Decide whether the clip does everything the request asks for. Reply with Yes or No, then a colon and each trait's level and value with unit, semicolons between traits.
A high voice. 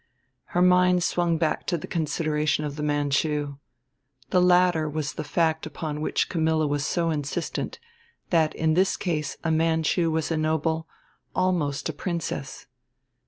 No: medium, 160 Hz